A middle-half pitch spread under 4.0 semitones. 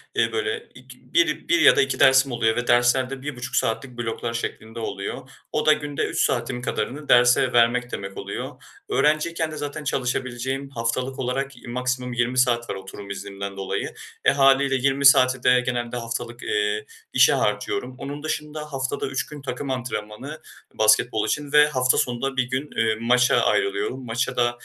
Yes: average, 2.7 semitones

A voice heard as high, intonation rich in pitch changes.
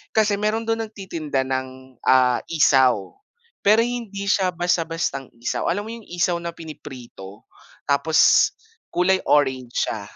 No: medium, 165 Hz; wide, 7.2 semitones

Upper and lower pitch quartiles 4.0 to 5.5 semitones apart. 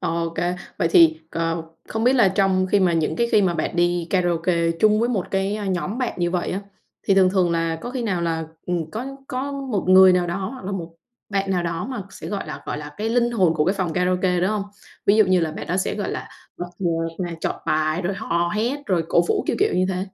No: average, 3.2 semitones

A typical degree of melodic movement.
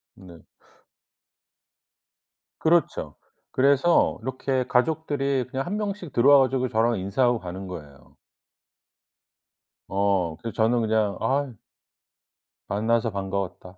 No: wide, 5.7 semitones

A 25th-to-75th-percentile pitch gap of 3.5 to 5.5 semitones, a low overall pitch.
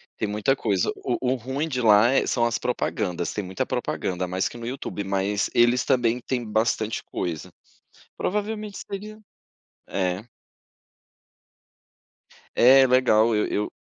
Yes: average, 4.2 semitones; low, 115 Hz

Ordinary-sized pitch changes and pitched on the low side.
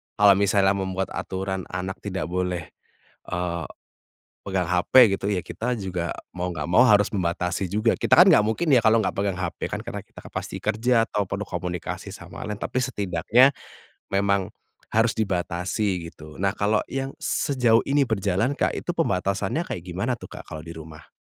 Yes: average, 3.5 semitones; very low, 95 Hz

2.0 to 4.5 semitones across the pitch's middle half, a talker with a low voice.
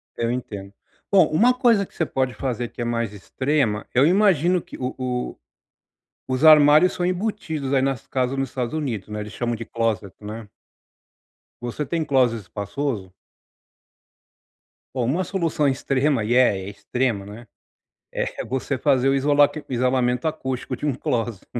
Yes: average, 4.2 semitones; low, 130 Hz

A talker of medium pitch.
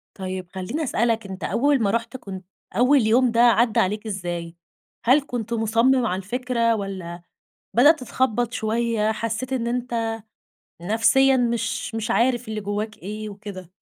No: high, 225 Hz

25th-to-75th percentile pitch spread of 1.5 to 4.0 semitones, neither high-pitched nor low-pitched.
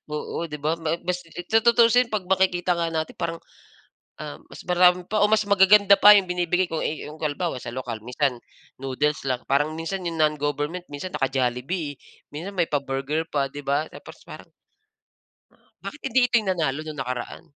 No: average, 4.4 semitones; medium, 165 Hz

